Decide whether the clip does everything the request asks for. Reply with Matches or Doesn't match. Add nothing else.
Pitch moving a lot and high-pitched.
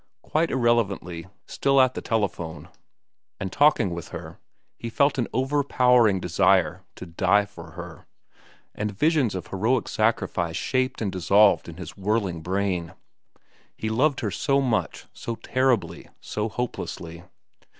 Doesn't match